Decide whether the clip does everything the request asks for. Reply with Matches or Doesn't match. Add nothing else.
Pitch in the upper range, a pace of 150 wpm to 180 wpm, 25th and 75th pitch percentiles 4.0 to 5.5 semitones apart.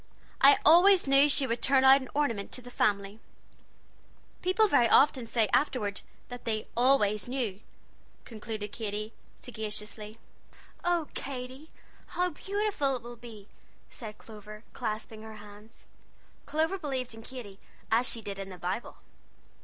Doesn't match